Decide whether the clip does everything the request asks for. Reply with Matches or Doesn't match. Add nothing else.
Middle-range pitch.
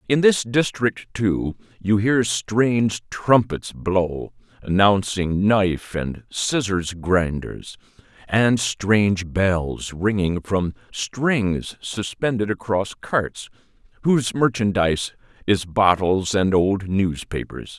Doesn't match